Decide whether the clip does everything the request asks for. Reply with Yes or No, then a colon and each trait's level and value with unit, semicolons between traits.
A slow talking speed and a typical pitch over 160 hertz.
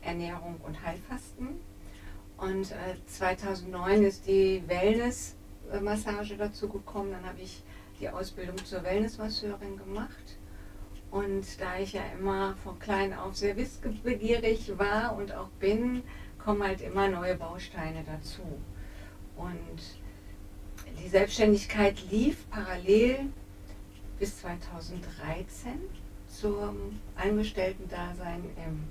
Yes: slow, 100 wpm; high, 190 Hz